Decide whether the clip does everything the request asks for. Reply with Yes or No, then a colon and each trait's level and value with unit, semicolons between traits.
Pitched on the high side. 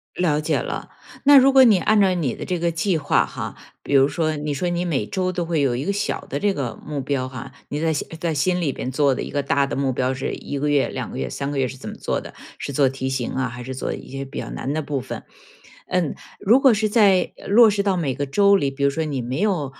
No: medium, 145 Hz